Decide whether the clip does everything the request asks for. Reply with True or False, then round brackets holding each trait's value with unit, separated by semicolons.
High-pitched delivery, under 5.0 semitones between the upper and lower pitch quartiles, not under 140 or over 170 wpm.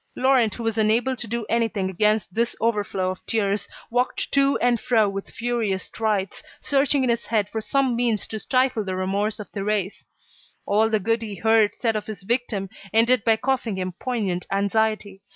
False (220 Hz; 2.9 semitones; 185 wpm)